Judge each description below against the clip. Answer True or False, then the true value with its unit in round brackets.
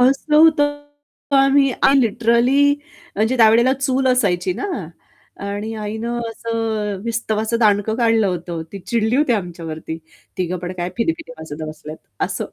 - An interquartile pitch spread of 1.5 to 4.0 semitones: False (4.8 semitones)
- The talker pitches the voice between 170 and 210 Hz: False (225 Hz)